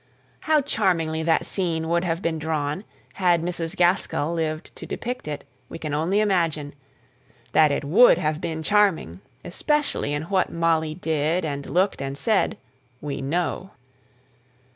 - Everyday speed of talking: Yes, average, 145 wpm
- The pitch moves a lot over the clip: No, average, 3.2 semitones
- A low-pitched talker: No, medium, 165 Hz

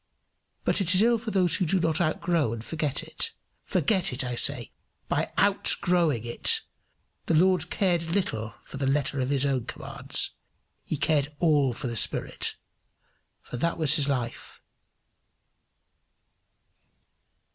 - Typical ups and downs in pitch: Yes, average, 5.0 semitones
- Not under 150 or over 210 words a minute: No, average, 140 wpm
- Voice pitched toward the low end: No, medium, 155 Hz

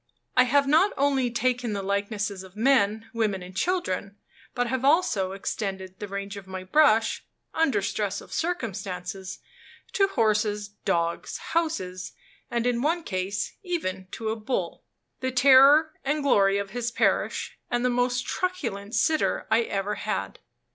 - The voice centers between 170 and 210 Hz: No, high, 225 Hz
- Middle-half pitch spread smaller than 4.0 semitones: No, average, 5.3 semitones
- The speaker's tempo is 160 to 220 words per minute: No, average, 150 wpm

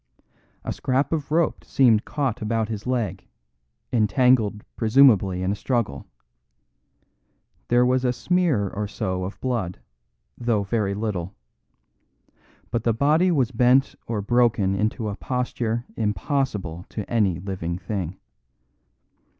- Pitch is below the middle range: Yes, low, 110 Hz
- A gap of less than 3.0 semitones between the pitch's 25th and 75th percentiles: No, average, 4.2 semitones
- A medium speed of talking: No, slow, 125 wpm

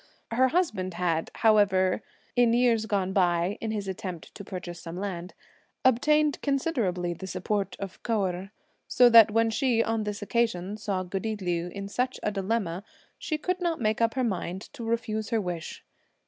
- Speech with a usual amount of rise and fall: Yes, average, 3.9 semitones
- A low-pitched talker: No, high, 210 Hz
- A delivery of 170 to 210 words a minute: Yes, average, 175 wpm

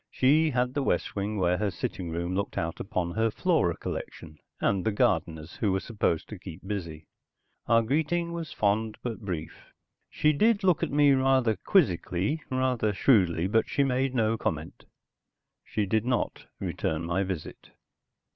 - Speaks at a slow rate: No, average, 165 wpm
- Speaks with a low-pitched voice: Yes, low, 110 Hz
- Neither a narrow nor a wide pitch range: No, wide, 6.5 semitones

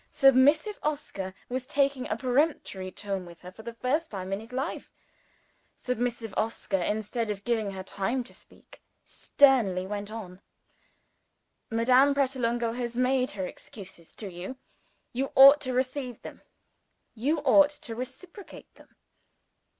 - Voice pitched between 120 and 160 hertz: No, high, 240 Hz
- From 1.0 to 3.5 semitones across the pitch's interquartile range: No, average, 4.7 semitones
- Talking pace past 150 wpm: No, average, 140 wpm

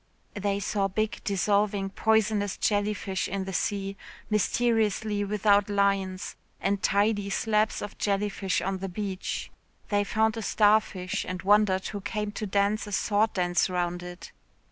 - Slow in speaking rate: No, average, 145 wpm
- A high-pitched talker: Yes, high, 205 Hz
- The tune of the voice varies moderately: No, narrow, 1.6 semitones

